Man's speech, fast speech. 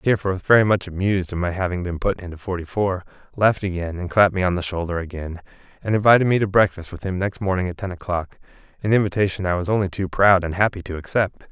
Yes: male; fast, 225 wpm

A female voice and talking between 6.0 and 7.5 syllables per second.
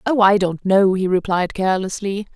No: female; 5.1 syllables/s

